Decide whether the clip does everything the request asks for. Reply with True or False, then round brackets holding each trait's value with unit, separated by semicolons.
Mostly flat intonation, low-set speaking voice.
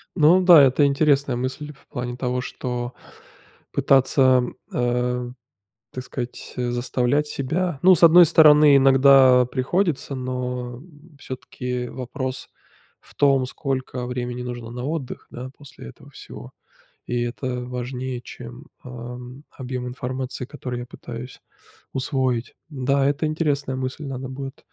True (2.1 semitones; 130 Hz)